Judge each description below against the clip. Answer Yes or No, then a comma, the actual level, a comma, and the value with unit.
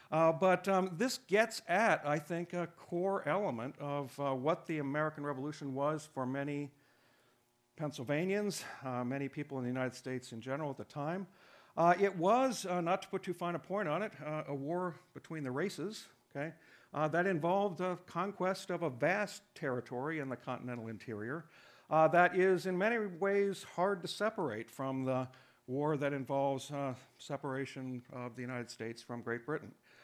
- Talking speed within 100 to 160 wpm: No, average, 180 wpm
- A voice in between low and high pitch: Yes, medium, 150 Hz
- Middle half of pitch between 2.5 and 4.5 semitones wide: No, wide, 5.4 semitones